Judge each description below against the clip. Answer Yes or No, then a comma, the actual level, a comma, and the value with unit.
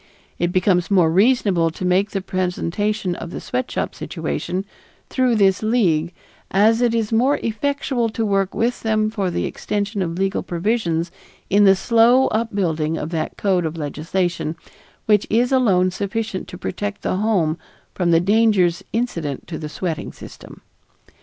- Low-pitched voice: No, high, 195 Hz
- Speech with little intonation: No, average, 4.3 semitones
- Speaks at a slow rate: No, average, 155 wpm